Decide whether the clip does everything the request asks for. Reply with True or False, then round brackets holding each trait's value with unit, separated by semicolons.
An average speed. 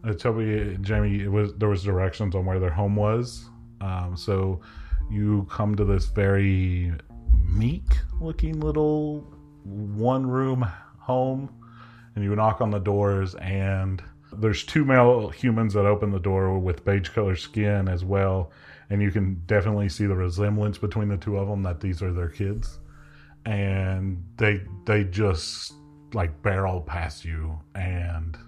True (150 wpm)